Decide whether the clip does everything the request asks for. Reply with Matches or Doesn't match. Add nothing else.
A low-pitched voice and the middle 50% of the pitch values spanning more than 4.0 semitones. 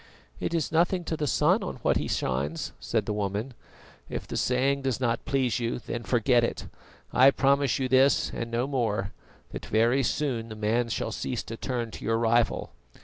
Doesn't match